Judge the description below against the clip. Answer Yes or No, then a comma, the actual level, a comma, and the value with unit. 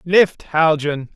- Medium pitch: Yes, medium, 160 Hz